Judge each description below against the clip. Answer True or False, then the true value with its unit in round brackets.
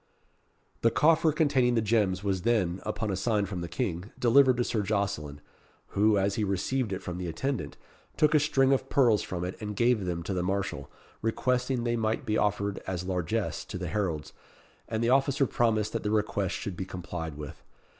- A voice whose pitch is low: True (105 Hz)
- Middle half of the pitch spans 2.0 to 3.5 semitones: False (4.8 semitones)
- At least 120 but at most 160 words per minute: False (195 wpm)